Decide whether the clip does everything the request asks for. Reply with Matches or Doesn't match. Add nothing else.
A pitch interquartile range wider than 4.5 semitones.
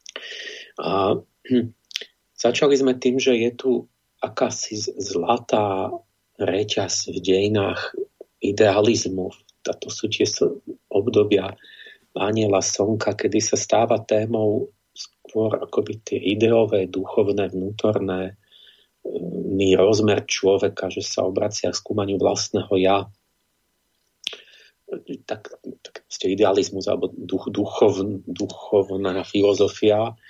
Matches